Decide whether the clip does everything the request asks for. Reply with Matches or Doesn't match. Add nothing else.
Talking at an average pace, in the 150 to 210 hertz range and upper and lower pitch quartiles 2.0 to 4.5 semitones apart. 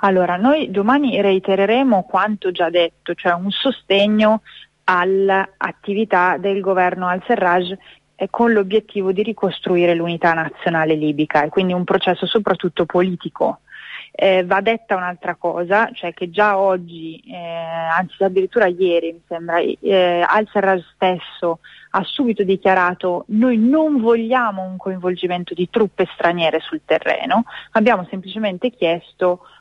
Matches